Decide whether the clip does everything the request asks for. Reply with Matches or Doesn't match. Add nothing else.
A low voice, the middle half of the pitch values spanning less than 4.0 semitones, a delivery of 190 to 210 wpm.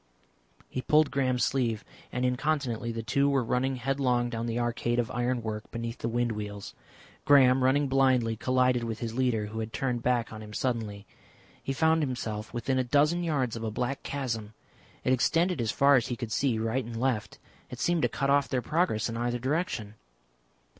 Matches